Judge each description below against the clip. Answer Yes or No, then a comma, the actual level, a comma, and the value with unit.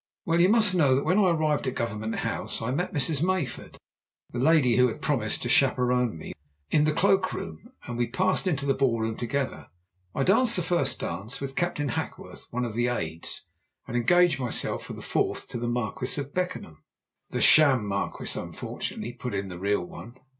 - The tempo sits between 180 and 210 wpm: Yes, average, 195 wpm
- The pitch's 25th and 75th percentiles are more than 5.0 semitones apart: Yes, wide, 5.6 semitones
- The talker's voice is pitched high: No, low, 130 Hz